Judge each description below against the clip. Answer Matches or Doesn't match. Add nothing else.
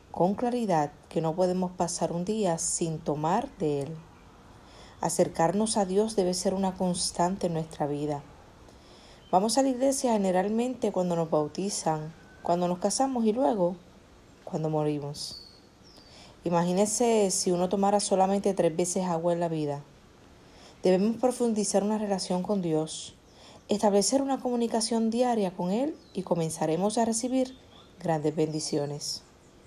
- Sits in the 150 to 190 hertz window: Matches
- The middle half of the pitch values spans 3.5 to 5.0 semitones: Matches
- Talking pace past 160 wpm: Doesn't match